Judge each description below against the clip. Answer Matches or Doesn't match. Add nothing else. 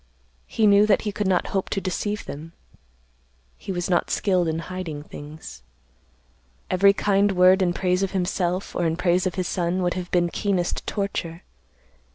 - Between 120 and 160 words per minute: Doesn't match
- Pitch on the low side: Doesn't match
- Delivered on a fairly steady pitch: Matches